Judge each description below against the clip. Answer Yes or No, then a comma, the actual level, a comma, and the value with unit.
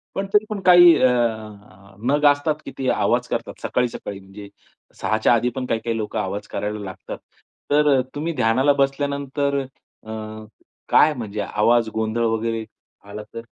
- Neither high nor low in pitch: No, low, 115 Hz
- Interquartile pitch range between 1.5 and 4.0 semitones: No, average, 4.7 semitones